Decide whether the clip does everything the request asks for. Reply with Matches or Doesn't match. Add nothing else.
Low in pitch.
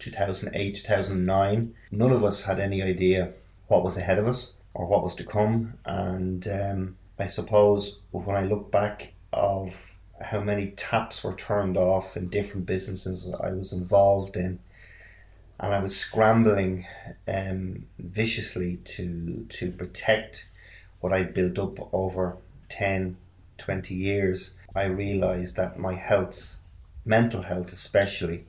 Matches